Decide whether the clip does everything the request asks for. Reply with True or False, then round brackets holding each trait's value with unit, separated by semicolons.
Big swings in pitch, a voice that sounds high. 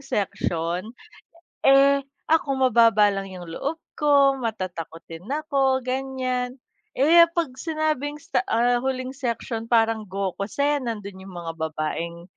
True (6.1 semitones; 240 Hz)